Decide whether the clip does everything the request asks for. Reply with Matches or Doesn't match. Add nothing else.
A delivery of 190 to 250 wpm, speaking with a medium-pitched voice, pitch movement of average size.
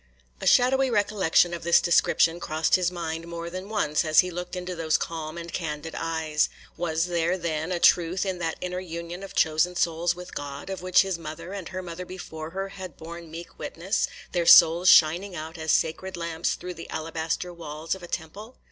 Doesn't match